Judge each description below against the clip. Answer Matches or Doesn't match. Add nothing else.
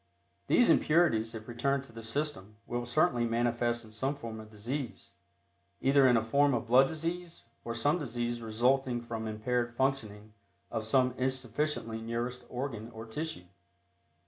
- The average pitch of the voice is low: Matches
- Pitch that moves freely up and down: Doesn't match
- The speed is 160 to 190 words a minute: Doesn't match